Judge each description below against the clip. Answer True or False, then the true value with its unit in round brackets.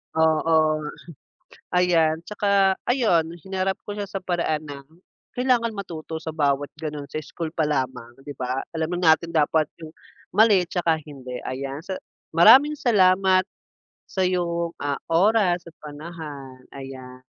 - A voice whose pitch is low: False (165 Hz)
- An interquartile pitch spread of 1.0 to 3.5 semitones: False (4.2 semitones)